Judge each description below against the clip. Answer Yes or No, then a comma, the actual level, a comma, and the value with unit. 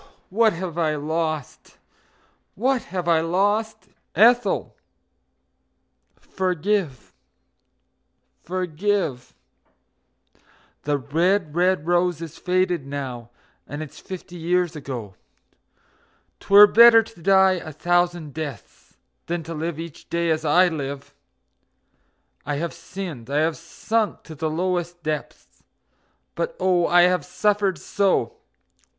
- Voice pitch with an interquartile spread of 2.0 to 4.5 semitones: Yes, average, 3.4 semitones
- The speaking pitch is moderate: Yes, medium, 175 Hz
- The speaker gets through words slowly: Yes, slow, 110 wpm